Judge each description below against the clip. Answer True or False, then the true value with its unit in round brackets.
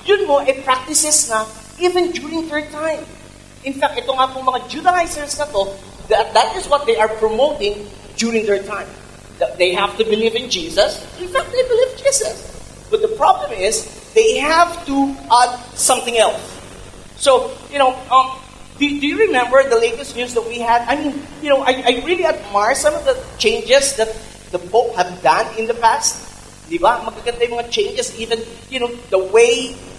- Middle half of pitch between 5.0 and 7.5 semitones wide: True (5.5 semitones)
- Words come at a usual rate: True (180 wpm)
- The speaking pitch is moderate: False (260 Hz)